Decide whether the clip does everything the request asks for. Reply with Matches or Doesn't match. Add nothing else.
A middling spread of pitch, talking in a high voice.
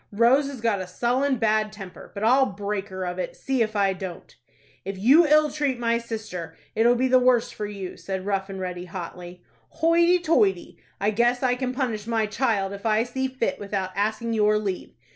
Matches